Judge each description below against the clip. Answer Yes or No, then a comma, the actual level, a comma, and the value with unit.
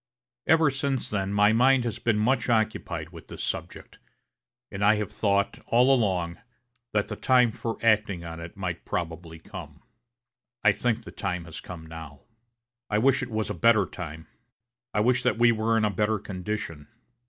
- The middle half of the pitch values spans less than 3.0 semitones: No, average, 4.9 semitones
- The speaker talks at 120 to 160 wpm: No, average, 175 wpm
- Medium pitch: No, low, 105 Hz